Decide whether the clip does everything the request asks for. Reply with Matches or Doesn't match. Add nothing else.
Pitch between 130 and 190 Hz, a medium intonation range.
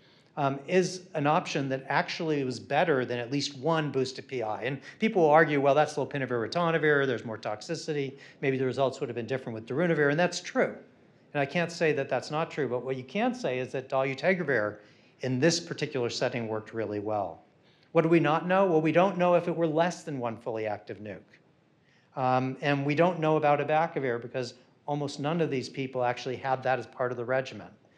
Matches